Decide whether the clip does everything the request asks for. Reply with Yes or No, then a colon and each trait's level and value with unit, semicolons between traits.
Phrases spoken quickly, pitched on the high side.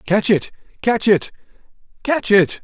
No: slow, 135 wpm; high, 205 Hz